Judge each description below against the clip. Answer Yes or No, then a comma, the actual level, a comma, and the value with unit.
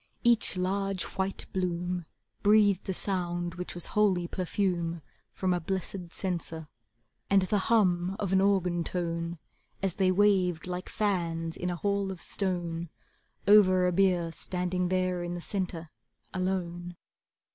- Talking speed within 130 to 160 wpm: Yes, average, 140 wpm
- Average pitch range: No, narrow, 1.9 semitones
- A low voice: No, medium, 180 Hz